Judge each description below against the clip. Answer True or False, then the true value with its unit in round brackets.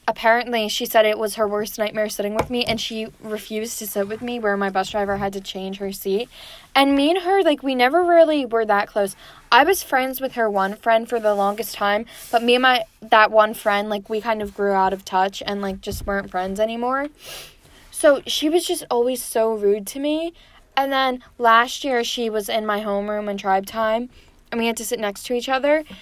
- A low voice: False (225 Hz)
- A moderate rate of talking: False (230 wpm)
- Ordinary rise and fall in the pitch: True (3.2 semitones)